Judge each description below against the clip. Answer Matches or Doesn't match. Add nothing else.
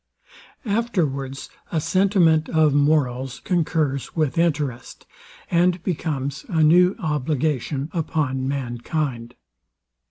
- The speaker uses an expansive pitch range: Doesn't match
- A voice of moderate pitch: Matches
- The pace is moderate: Doesn't match